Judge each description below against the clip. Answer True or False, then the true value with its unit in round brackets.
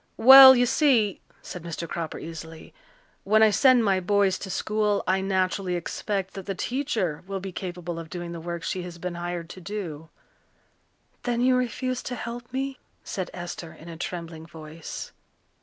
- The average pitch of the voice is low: False (185 Hz)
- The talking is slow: False (175 wpm)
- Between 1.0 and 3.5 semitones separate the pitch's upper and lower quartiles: False (4.4 semitones)